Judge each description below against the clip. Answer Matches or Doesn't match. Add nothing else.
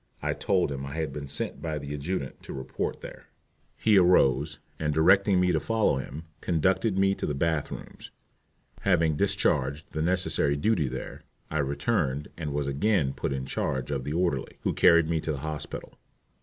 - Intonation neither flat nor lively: Matches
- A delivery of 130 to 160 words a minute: Doesn't match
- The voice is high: Doesn't match